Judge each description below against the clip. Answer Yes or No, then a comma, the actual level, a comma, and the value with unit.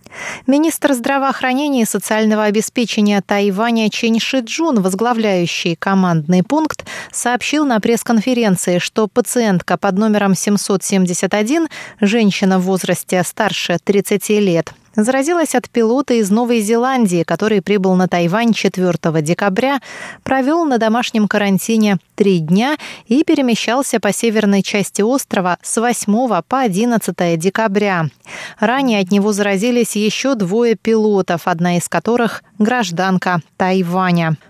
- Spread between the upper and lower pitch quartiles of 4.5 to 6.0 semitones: No, average, 4.0 semitones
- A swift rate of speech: No, average, 115 wpm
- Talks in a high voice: Yes, high, 215 Hz